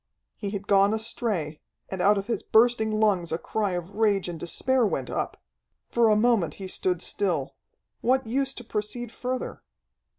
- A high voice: Yes, high, 210 Hz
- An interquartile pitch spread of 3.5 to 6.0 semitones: Yes, average, 3.8 semitones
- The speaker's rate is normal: Yes, average, 170 wpm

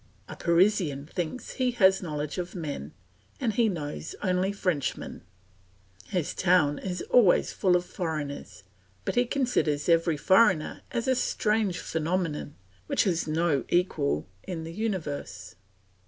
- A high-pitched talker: No, medium, 175 Hz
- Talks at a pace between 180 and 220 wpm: No, average, 140 wpm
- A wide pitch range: No, average, 4.3 semitones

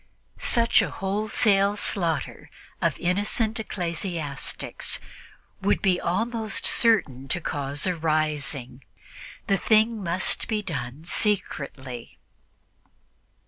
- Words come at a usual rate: No, slow, 95 wpm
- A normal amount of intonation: No, wide, 6.0 semitones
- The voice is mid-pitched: Yes, medium, 180 Hz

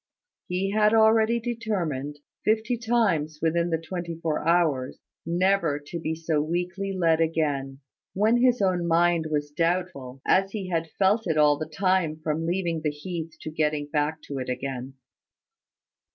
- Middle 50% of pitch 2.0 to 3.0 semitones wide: No, average, 4.0 semitones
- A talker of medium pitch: Yes, medium, 165 Hz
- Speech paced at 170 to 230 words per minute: No, average, 155 wpm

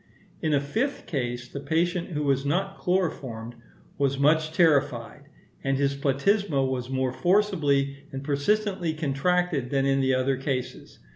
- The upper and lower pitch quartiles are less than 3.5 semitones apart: No, average, 4.4 semitones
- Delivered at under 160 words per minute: Yes, average, 145 wpm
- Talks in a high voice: No, medium, 140 Hz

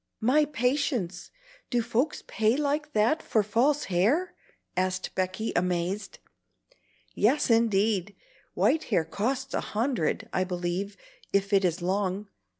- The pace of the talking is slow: Yes, slow, 125 wpm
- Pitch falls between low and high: No, high, 210 Hz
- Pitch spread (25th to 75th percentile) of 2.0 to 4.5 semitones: No, wide, 5.5 semitones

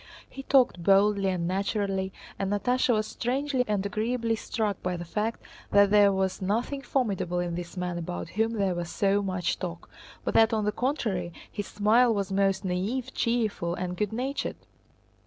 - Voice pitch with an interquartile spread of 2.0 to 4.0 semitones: Yes, average, 3.5 semitones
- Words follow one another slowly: No, average, 175 wpm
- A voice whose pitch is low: No, high, 200 Hz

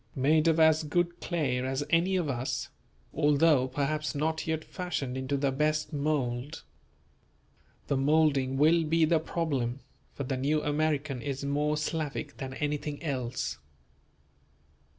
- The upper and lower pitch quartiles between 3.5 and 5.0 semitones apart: No, average, 2.8 semitones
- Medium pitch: Yes, medium, 150 Hz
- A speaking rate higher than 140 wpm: No, slow, 135 wpm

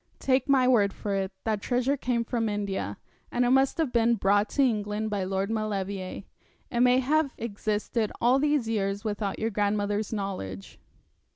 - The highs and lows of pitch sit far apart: No, average, 3.6 semitones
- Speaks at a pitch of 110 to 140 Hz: No, high, 215 Hz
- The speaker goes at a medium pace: Yes, average, 170 wpm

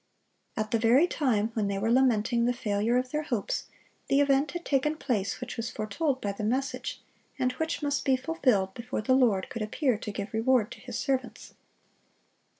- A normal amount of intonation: Yes, average, 3.9 semitones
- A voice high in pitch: Yes, high, 245 Hz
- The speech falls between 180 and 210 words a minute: Yes, average, 190 wpm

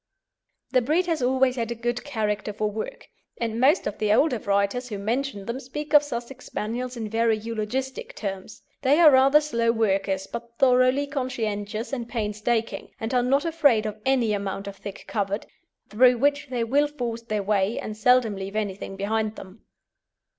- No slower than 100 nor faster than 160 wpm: No, average, 175 wpm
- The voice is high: Yes, high, 235 Hz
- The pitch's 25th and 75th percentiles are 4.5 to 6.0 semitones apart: No, average, 3.7 semitones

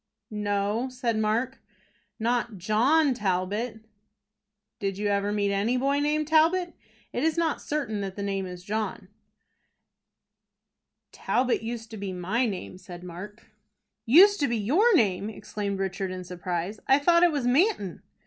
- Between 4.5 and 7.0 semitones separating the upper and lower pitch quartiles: Yes, average, 5.2 semitones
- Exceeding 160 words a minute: No, average, 150 wpm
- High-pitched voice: Yes, high, 220 Hz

